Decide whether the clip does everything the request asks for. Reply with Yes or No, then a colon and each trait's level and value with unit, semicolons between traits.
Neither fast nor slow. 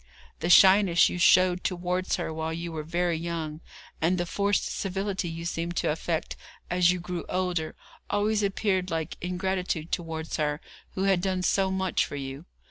Yes: average, 170 wpm